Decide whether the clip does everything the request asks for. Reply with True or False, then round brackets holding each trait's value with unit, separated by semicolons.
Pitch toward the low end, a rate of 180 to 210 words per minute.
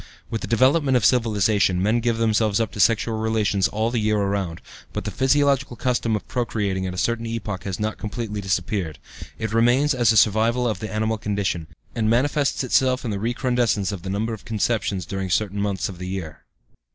True (110 Hz; 200 wpm)